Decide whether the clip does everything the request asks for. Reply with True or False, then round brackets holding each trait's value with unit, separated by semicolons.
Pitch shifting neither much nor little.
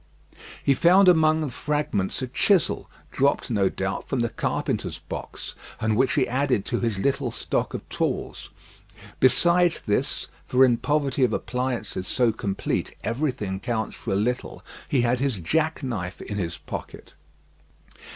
True (4.9 semitones)